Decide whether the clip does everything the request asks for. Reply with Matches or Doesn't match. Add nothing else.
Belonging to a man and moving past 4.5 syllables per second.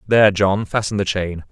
Matches